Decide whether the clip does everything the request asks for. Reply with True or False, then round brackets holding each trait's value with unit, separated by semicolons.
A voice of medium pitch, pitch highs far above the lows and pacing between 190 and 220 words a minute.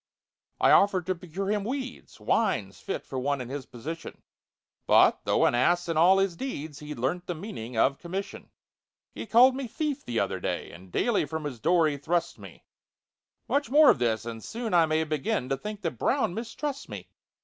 True (170 Hz; 7.7 semitones; 195 wpm)